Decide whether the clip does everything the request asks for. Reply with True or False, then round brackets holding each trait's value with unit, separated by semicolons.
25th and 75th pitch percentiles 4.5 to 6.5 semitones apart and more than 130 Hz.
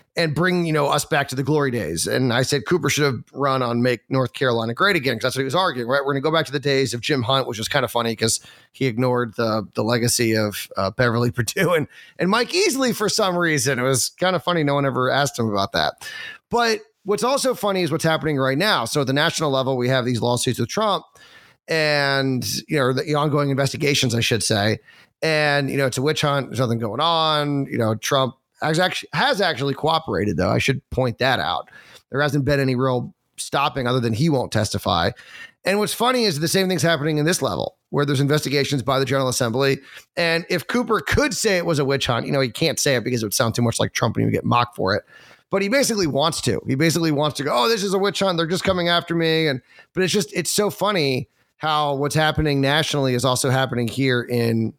True (4.8 semitones; 140 Hz)